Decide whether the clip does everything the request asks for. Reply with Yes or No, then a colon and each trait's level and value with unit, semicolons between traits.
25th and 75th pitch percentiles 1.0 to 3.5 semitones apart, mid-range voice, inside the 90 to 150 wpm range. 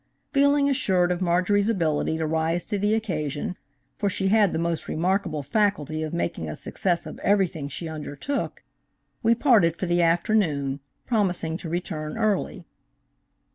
No: average, 4.6 semitones; medium, 175 Hz; average, 140 wpm